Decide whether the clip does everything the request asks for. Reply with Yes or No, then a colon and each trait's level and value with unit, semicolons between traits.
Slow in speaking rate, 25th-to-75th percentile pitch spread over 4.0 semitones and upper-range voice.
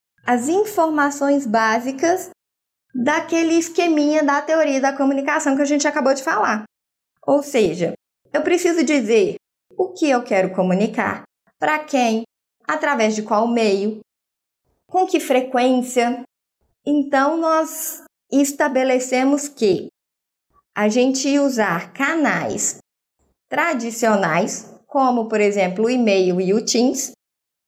Yes: slow, 110 wpm; average, 5.1 semitones; very high, 275 Hz